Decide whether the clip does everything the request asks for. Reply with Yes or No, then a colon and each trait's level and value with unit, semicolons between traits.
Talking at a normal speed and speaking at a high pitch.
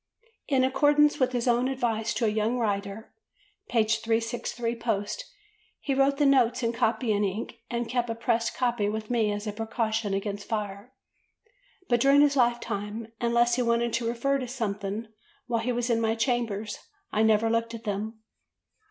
Yes: average, 170 wpm; high, 230 Hz